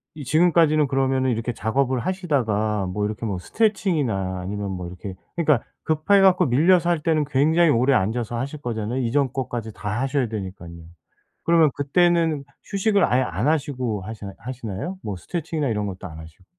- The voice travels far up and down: Yes, wide, 6.9 semitones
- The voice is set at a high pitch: No, low, 130 Hz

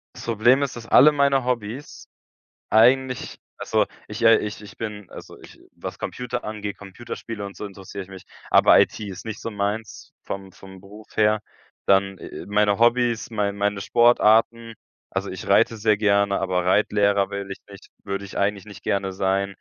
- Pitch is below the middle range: Yes, low, 105 Hz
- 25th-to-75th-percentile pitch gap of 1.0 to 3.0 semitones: Yes, narrow, 2.6 semitones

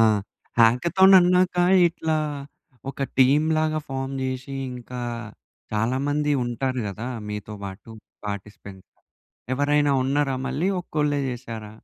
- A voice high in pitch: No, low, 135 Hz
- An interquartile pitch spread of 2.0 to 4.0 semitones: No, average, 4.5 semitones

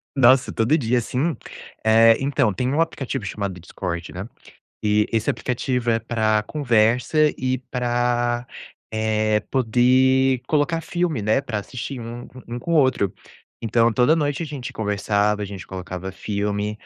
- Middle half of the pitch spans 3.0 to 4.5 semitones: Yes, average, 3.7 semitones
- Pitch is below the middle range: Yes, low, 120 Hz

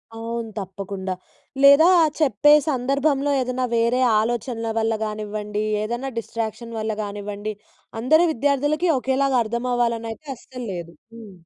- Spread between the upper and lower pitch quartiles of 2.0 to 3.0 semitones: No, average, 3.8 semitones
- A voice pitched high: Yes, high, 235 Hz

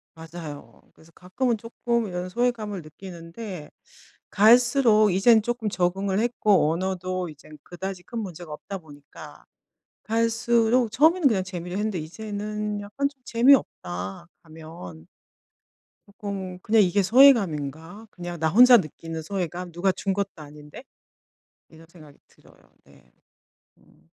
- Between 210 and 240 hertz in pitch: No, high, 190 Hz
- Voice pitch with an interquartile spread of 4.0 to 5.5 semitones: Yes, average, 5.2 semitones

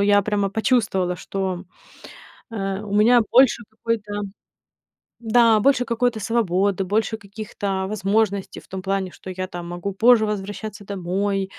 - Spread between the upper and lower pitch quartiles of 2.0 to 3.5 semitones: Yes, narrow, 2.4 semitones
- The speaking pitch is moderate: No, high, 205 Hz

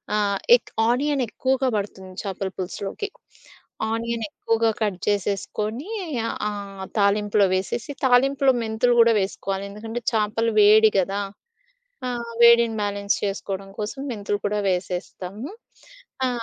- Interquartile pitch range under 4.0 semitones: Yes, average, 2.8 semitones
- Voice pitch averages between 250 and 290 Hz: No, high, 210 Hz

